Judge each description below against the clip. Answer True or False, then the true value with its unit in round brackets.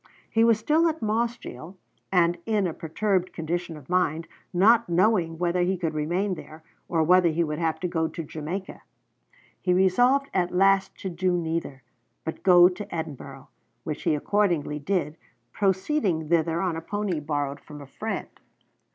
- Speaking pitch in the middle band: True (175 Hz)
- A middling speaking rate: True (170 wpm)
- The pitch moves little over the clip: False (3.5 semitones)